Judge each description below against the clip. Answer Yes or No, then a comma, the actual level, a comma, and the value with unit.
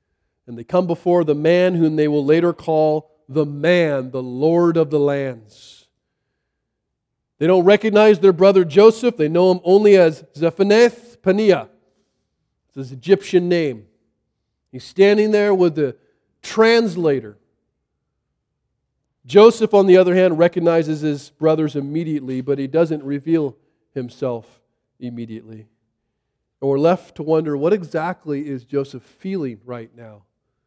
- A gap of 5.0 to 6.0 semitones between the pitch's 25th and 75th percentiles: Yes, average, 5.3 semitones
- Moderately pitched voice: Yes, medium, 155 Hz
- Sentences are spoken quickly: No, slow, 135 wpm